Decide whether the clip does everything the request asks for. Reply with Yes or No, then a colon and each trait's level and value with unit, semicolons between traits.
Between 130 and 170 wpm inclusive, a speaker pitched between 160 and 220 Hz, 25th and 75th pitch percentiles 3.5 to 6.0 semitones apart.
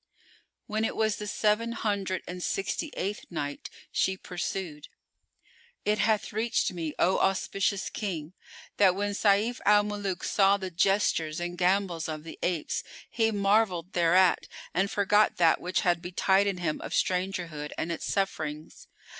No: average, 145 wpm; high, 190 Hz; average, 3.0 semitones